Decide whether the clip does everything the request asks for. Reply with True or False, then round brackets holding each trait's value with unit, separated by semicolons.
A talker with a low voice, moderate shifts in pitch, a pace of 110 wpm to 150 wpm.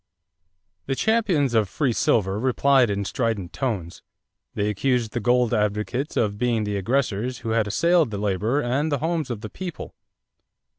False (115 Hz; 4.7 semitones; 165 wpm)